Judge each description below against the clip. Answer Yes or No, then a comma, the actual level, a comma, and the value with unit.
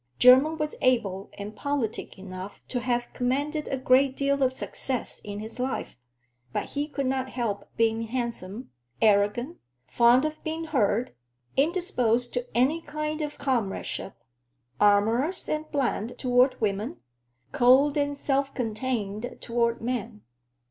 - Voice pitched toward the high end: Yes, very high, 250 Hz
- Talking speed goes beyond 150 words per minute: No, slow, 135 wpm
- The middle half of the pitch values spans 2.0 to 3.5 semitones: No, average, 4.0 semitones